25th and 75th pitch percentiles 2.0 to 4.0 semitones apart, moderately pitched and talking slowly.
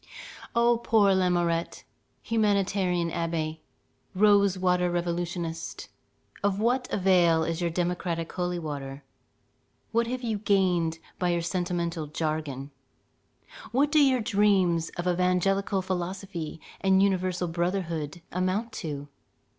Yes: average, 2.9 semitones; medium, 180 Hz; slow, 110 wpm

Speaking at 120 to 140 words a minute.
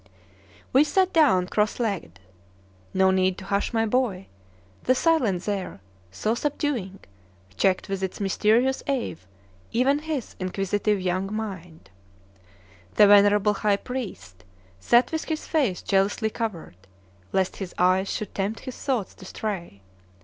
Yes: slow, 135 wpm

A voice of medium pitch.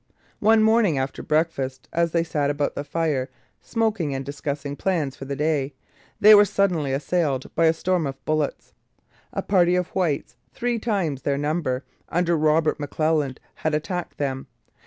Yes: medium, 155 Hz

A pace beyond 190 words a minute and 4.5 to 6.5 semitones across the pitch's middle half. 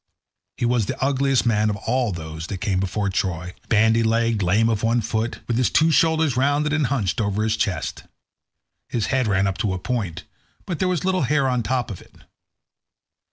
Yes: average, 200 wpm; average, 4.8 semitones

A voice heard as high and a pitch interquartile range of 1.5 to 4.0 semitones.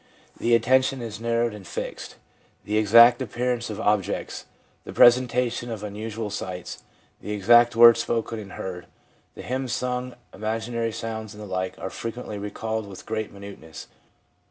No: low, 110 Hz; narrow, 2.4 semitones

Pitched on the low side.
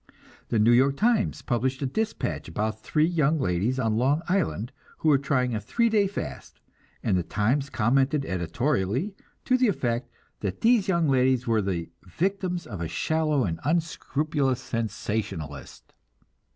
Yes: low, 130 Hz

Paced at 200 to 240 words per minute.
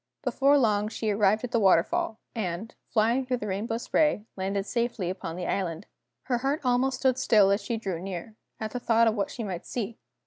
Yes: fast, 205 wpm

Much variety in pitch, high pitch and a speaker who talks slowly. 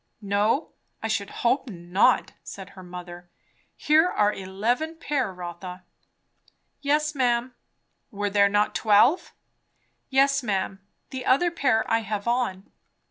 Yes: wide, 5.7 semitones; high, 220 Hz; slow, 125 wpm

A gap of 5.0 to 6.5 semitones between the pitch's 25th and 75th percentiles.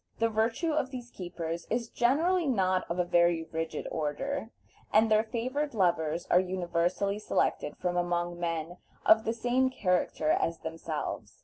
Yes: wide, 5.5 semitones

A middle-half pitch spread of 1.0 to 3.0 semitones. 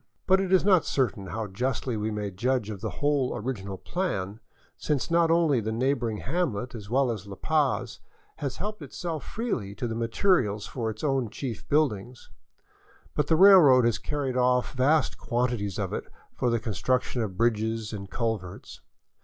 No: average, 5.3 semitones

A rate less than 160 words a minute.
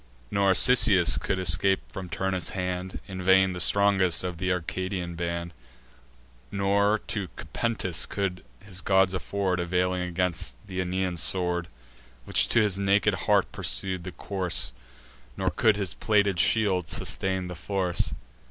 Yes: average, 145 wpm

